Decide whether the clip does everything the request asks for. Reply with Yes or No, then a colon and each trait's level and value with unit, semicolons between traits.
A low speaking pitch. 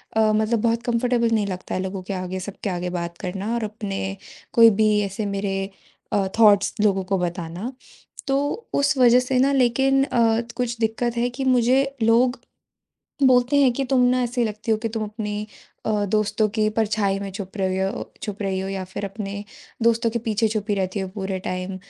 No: high, 215 Hz